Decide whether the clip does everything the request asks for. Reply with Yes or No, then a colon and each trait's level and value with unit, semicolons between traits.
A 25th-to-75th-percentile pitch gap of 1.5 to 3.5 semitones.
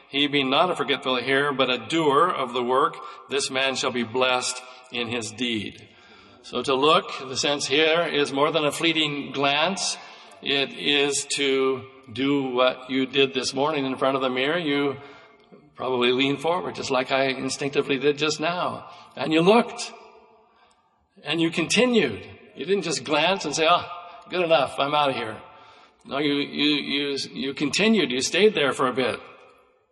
Yes: average, 3.2 semitones